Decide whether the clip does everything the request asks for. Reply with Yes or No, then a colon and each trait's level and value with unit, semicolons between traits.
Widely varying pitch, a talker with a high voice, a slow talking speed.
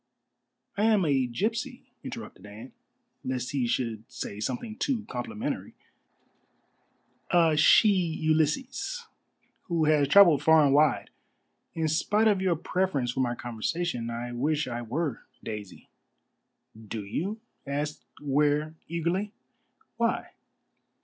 No: wide, 7.3 semitones; medium, 155 Hz; slow, 115 wpm